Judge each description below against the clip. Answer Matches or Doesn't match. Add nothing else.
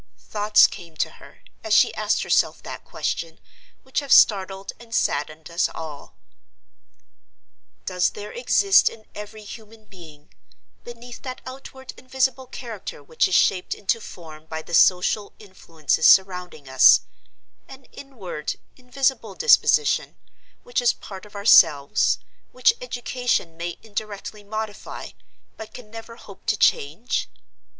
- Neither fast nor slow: Doesn't match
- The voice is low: Doesn't match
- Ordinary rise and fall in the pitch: Doesn't match